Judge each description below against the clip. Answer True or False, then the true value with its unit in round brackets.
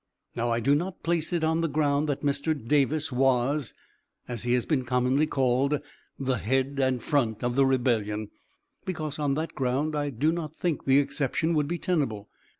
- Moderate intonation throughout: True (3.5 semitones)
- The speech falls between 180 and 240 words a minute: True (185 wpm)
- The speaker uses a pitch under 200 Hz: True (140 Hz)